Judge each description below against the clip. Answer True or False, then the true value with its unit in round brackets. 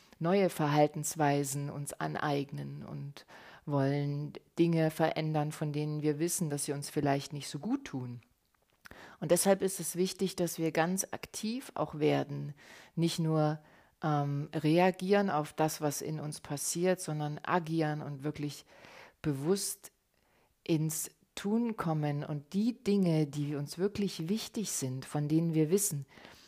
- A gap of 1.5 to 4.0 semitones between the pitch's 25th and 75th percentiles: True (3.3 semitones)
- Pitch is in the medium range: True (155 Hz)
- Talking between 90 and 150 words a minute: True (140 wpm)